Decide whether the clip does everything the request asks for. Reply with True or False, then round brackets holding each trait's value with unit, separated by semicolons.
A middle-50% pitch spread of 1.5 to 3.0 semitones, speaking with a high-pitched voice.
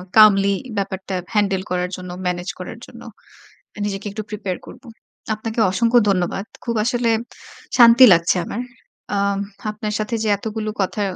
True (2.4 semitones; 205 Hz)